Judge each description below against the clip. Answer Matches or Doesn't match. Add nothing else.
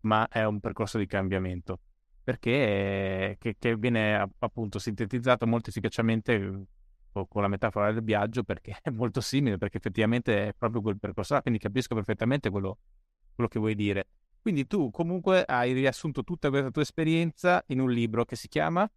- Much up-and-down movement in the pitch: Doesn't match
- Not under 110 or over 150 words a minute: Doesn't match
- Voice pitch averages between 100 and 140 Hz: Matches